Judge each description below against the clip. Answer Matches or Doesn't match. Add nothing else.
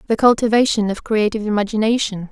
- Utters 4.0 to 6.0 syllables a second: Doesn't match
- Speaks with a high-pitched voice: Matches